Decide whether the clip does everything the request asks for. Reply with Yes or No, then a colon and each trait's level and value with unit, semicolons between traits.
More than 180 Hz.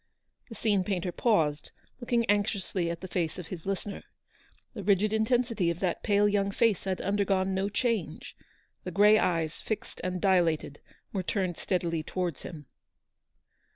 Yes: high, 190 Hz